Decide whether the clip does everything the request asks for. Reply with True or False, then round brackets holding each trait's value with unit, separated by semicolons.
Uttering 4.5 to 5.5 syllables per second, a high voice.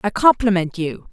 True (5.0 syllables/s; 195 Hz)